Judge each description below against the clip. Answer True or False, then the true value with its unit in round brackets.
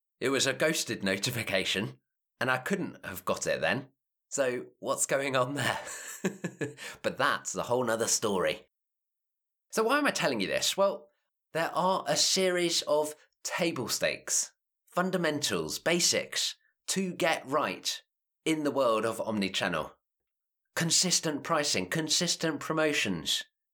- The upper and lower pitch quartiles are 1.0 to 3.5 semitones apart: False (4.5 semitones)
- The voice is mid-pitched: True (155 Hz)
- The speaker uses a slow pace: True (130 wpm)